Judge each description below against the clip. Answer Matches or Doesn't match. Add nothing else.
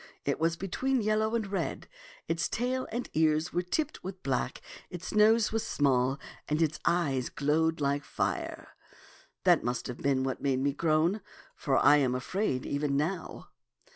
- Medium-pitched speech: Matches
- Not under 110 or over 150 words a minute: Doesn't match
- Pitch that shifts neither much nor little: Doesn't match